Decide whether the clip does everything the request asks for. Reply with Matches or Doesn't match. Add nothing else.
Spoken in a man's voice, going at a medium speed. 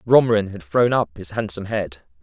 Matches